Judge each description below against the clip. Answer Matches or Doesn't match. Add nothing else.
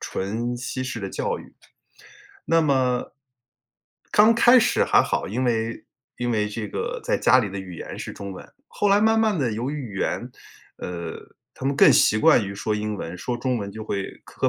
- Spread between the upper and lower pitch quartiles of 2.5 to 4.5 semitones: Doesn't match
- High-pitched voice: Doesn't match